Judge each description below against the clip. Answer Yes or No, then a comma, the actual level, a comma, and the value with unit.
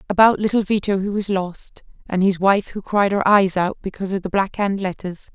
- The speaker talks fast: Yes, fast, 225 wpm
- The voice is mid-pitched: No, high, 195 Hz